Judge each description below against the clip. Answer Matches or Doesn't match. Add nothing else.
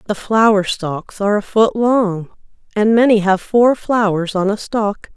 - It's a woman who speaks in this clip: Matches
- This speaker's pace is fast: Doesn't match